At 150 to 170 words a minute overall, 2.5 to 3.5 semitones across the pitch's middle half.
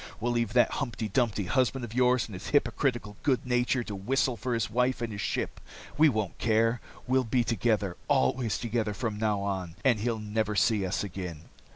No: average, 195 wpm; average, 3.1 semitones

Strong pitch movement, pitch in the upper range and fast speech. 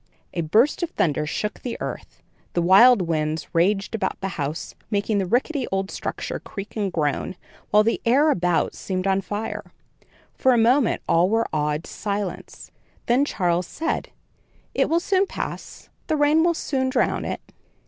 No: wide, 6.3 semitones; high, 205 Hz; average, 170 wpm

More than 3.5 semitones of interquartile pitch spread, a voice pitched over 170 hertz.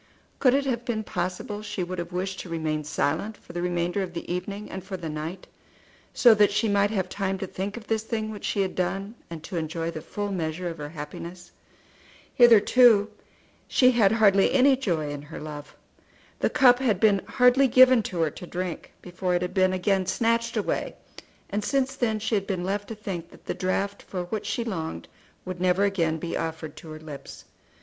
Yes: average, 4.0 semitones; high, 190 Hz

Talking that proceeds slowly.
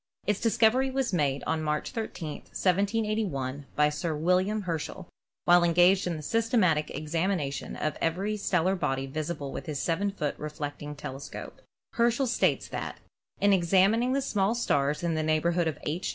No: average, 165 wpm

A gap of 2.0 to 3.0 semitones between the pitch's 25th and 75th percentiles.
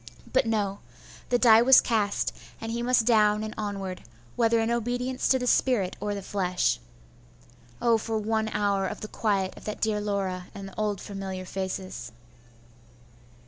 Yes: average, 2.7 semitones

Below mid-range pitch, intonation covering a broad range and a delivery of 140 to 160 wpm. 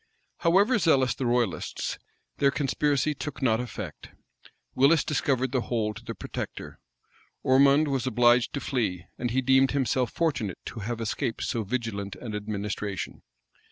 No: low, 125 Hz; average, 3.7 semitones; average, 145 wpm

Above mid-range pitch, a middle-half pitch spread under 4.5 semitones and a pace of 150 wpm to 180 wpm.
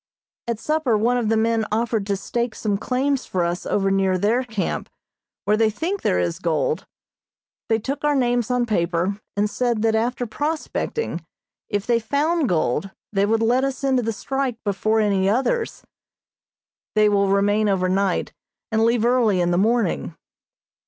Yes: high, 220 Hz; average, 3.8 semitones; average, 170 wpm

